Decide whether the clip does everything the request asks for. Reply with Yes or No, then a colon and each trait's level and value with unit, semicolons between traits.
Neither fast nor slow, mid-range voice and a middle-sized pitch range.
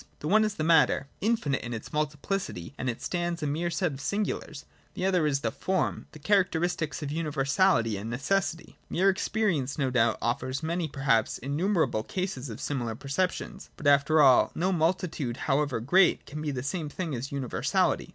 Yes: average, 180 wpm; medium, 150 Hz; average, 5.0 semitones